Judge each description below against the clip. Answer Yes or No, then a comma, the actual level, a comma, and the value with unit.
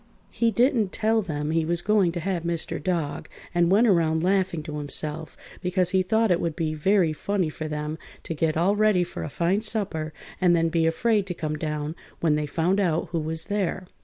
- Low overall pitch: No, medium, 170 Hz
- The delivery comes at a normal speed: No, fast, 210 wpm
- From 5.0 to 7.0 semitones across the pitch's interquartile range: No, average, 3.7 semitones